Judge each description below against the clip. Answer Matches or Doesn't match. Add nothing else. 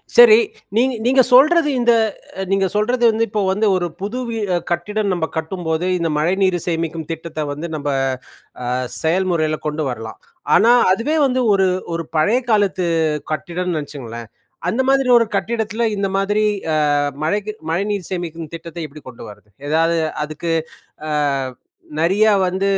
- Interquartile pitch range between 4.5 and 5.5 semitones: Matches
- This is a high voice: Doesn't match